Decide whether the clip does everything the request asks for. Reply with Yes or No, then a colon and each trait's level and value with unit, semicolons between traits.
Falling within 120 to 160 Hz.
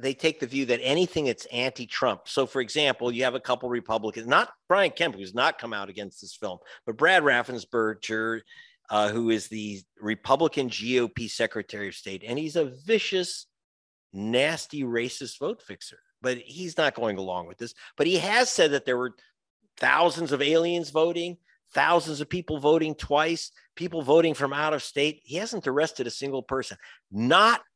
Yes: low, 135 Hz